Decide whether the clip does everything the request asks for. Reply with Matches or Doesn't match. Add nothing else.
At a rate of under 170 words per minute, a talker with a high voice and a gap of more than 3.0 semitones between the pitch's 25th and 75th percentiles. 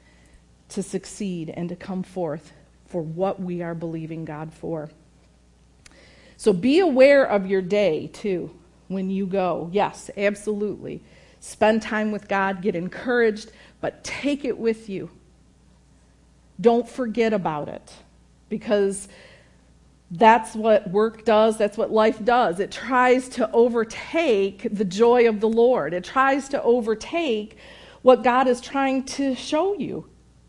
Matches